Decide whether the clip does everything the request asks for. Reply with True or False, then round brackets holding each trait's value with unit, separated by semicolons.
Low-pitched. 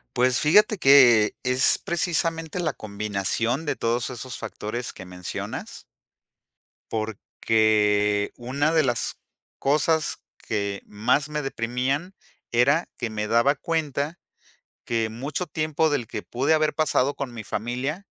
True (125 Hz)